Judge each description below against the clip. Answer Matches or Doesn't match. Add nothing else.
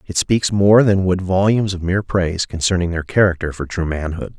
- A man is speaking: Matches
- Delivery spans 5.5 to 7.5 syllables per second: Matches